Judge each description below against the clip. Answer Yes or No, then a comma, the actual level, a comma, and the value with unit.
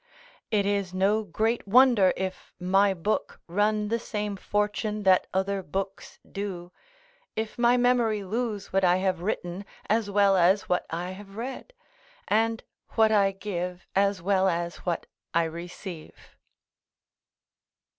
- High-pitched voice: Yes, high, 200 Hz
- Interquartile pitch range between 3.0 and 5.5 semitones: No, narrow, 2.5 semitones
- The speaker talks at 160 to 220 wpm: No, slow, 135 wpm